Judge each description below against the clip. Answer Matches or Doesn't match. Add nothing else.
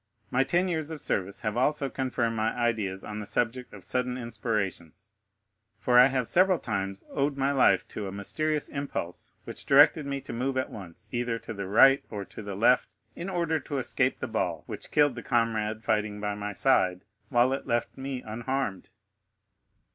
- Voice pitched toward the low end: Matches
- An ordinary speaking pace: Matches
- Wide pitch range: Doesn't match